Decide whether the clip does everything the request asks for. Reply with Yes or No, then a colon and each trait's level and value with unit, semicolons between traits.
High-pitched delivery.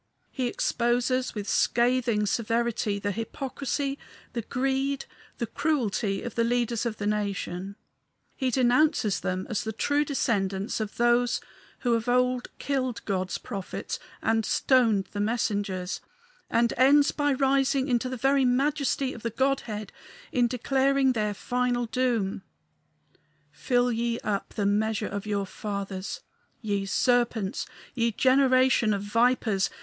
Yes: high, 235 Hz